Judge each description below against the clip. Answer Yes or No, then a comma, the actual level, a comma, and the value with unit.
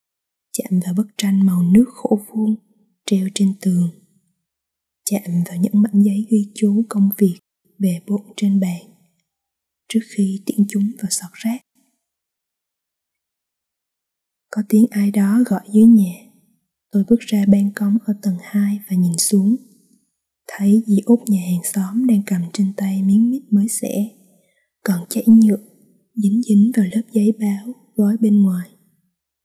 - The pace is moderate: No, slow, 155 wpm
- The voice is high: Yes, high, 205 Hz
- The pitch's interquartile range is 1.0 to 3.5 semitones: Yes, narrow, 2.6 semitones